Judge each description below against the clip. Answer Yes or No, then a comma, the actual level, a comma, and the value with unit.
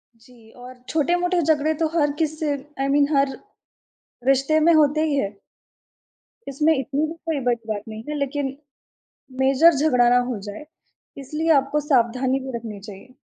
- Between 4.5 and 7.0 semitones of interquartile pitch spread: No, average, 3.7 semitones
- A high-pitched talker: Yes, very high, 275 Hz